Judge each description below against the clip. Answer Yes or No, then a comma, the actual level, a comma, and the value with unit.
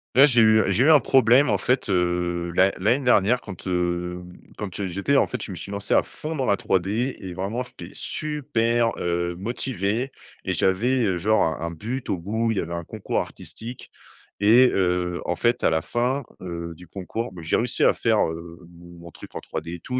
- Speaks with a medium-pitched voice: No, low, 100 Hz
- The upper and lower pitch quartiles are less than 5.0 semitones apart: No, wide, 5.6 semitones